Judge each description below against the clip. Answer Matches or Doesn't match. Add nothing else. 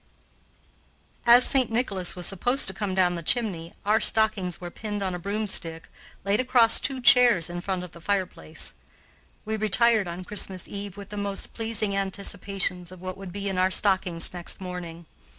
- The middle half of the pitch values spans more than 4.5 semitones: Doesn't match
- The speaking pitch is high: Matches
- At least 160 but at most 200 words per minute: Matches